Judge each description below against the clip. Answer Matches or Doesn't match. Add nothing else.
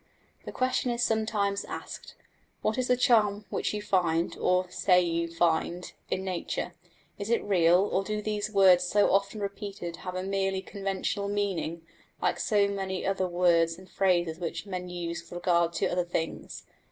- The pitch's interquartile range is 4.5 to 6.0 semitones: Doesn't match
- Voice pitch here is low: Doesn't match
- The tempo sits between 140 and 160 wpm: Doesn't match